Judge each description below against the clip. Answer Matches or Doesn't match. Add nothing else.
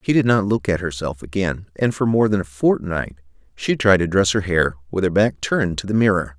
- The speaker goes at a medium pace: Doesn't match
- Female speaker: Doesn't match